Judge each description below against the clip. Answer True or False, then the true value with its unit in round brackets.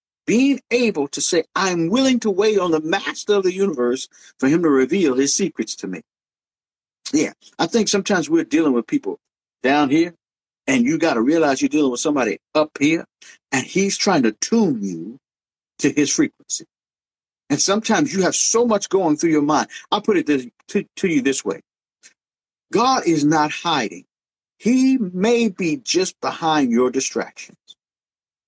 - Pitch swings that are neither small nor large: False (7.8 semitones)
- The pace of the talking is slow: False (175 wpm)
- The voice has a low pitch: False (190 Hz)